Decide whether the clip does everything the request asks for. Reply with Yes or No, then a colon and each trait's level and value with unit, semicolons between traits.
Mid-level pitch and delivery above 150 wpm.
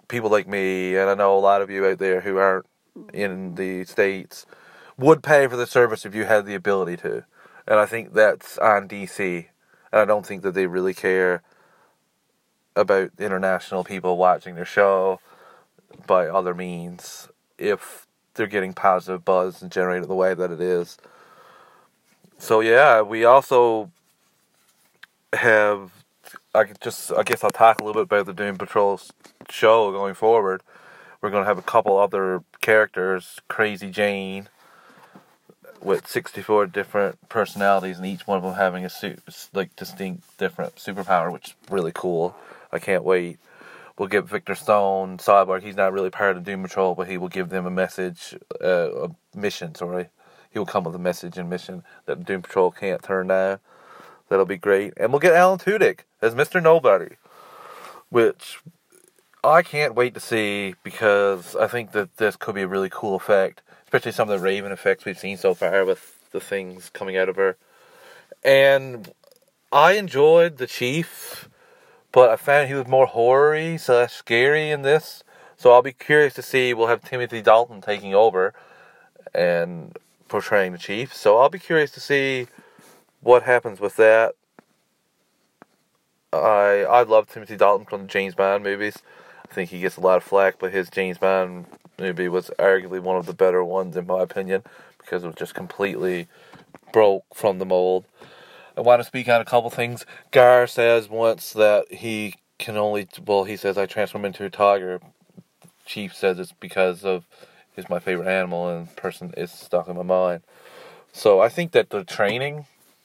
No: low, 100 Hz; average, 175 wpm